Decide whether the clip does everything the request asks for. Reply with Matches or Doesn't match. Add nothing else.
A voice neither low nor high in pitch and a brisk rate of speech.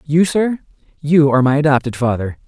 Doesn't match